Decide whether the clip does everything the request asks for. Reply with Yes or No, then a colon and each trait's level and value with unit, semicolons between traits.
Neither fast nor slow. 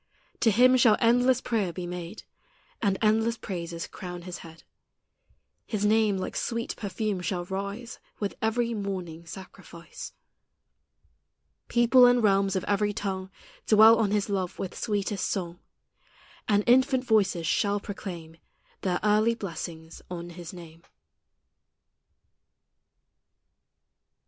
No: slow, 120 wpm